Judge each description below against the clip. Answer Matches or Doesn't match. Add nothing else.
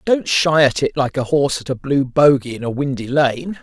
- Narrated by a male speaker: Matches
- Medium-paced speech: Doesn't match